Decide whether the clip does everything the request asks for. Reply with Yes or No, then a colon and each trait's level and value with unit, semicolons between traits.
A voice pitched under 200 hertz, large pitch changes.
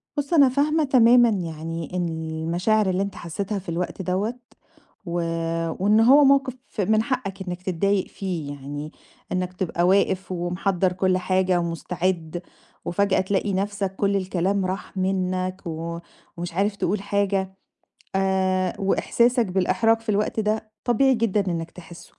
No: high, 190 Hz; average, 2.9 semitones